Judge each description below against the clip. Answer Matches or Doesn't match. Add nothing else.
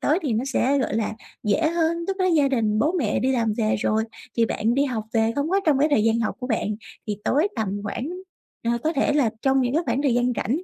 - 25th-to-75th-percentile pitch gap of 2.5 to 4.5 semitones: Doesn't match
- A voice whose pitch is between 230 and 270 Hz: Matches